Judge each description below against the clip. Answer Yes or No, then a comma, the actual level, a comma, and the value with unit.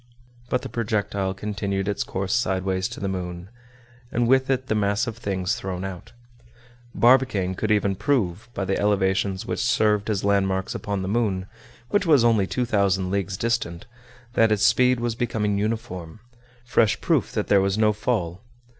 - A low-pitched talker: Yes, low, 100 Hz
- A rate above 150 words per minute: Yes, average, 165 wpm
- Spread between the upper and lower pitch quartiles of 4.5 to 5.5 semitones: No, average, 3.6 semitones